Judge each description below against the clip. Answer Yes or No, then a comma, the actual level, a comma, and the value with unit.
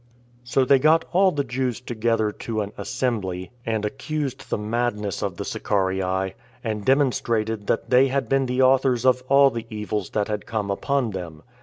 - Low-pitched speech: Yes, low, 115 Hz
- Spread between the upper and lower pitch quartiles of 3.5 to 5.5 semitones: Yes, average, 4.0 semitones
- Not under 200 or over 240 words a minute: No, average, 175 wpm